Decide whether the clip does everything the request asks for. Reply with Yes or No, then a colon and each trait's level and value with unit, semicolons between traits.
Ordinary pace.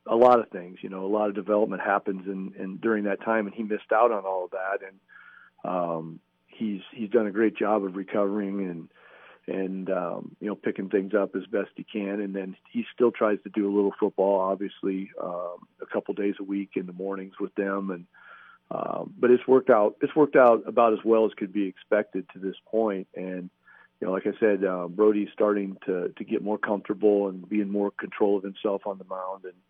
No: fast, 230 wpm